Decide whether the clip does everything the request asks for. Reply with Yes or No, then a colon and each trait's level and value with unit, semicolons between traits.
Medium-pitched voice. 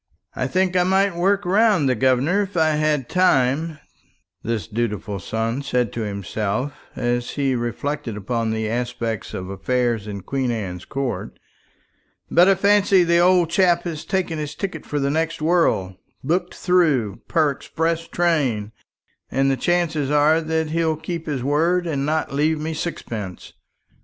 Yes: medium, 150 Hz